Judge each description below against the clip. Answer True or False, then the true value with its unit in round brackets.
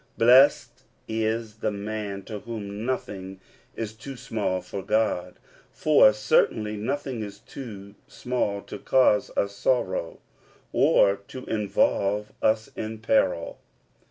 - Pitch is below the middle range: True (110 Hz)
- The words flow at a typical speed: False (120 wpm)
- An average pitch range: False (2.3 semitones)